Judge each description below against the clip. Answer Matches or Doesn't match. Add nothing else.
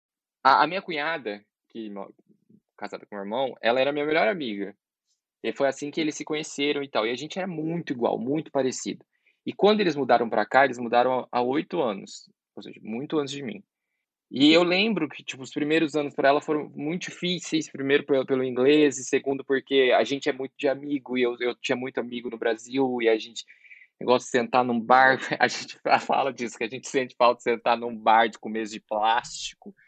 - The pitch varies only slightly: Doesn't match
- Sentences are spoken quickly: Matches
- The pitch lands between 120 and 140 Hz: Matches